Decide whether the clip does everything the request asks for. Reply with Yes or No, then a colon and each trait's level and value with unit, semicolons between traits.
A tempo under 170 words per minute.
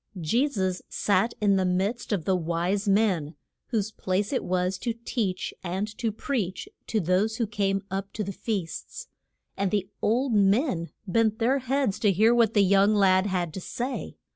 No: average, 180 wpm